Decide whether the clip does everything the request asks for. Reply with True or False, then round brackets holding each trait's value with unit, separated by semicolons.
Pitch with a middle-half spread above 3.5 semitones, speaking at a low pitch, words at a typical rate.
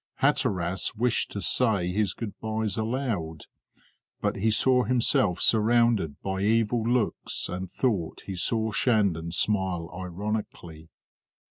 False (4.1 semitones; 105 Hz; 120 wpm)